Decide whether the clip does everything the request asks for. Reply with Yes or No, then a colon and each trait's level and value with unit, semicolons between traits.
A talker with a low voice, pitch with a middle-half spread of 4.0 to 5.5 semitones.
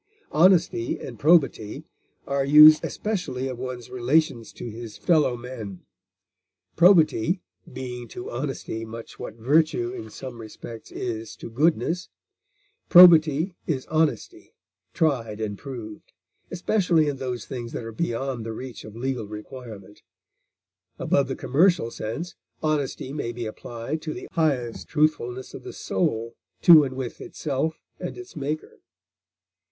Yes: low, 130 Hz; average, 5.1 semitones